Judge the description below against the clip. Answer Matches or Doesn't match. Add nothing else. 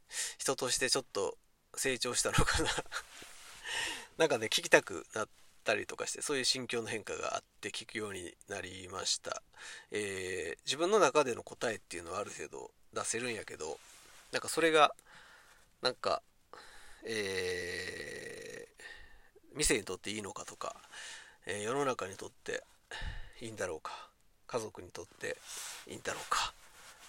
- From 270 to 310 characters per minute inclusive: Matches